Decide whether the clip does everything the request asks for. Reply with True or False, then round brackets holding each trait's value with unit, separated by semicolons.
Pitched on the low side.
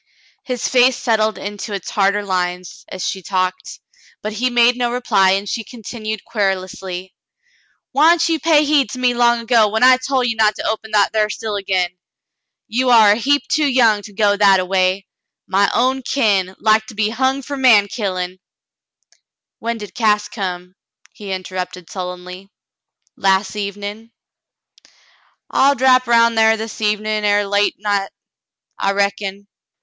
False (210 Hz)